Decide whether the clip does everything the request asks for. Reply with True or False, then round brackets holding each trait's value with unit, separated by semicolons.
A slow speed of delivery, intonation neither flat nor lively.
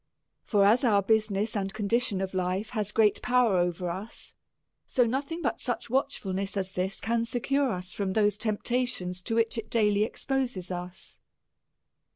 False (165 wpm; 3.6 semitones)